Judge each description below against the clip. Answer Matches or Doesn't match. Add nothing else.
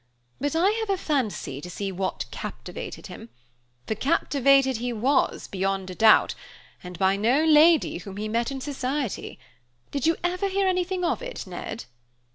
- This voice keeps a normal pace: Matches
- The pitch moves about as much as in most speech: Doesn't match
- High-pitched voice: Matches